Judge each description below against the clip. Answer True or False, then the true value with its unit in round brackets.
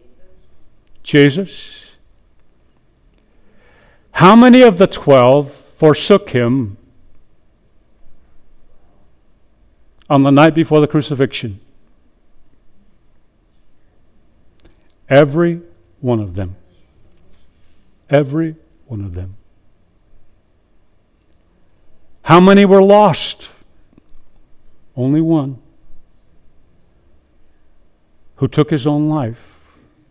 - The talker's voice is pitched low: True (105 Hz)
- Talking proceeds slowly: True (65 wpm)